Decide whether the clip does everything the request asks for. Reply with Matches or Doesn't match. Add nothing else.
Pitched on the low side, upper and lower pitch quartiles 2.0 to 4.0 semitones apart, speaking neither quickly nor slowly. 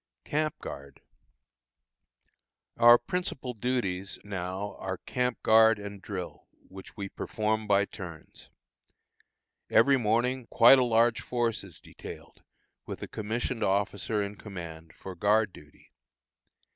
Doesn't match